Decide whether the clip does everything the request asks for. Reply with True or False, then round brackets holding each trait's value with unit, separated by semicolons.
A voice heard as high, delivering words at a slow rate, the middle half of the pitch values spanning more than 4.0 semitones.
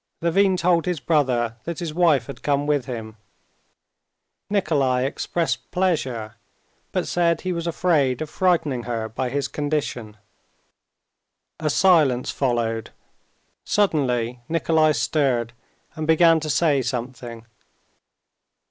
False (145 Hz; 115 wpm; 5.4 semitones)